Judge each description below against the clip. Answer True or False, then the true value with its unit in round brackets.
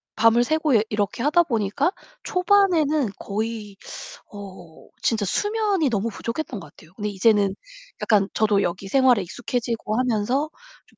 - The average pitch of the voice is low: False (225 Hz)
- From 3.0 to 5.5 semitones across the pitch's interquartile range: False (6.1 semitones)